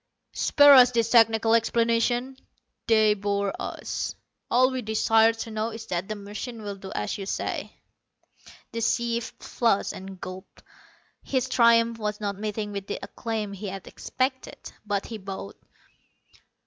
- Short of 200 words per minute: Yes, average, 150 wpm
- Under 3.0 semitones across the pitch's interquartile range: Yes, narrow, 2.5 semitones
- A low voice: No, high, 220 Hz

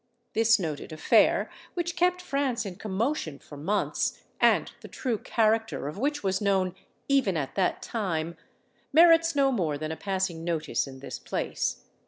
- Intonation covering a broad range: Yes, wide, 8.7 semitones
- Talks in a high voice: Yes, high, 200 Hz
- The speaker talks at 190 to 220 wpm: No, average, 160 wpm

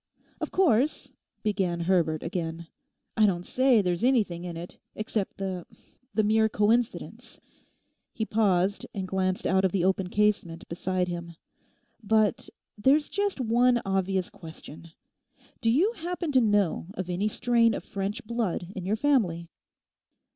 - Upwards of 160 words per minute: No, slow, 135 wpm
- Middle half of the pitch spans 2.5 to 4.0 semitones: No, average, 4.4 semitones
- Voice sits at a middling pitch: No, high, 200 Hz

